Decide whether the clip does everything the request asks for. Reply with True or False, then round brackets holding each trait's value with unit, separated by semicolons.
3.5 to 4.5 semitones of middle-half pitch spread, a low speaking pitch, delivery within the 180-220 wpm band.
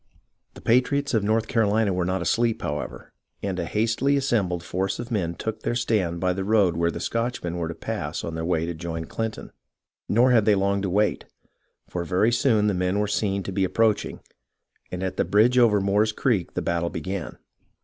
True (4.2 semitones; 100 Hz; 205 wpm)